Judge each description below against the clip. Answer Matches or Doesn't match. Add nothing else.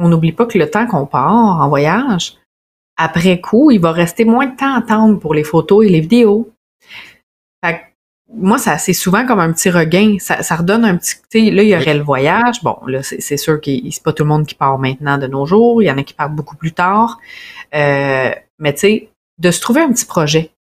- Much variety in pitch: Matches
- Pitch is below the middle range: Doesn't match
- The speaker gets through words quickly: Matches